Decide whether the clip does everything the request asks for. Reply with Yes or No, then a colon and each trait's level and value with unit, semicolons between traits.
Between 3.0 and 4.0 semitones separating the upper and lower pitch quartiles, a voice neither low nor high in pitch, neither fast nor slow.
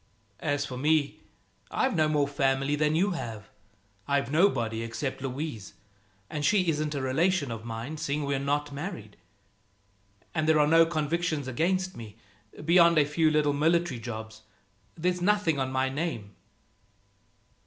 Yes: average, 3.7 semitones; medium, 145 Hz; average, 145 wpm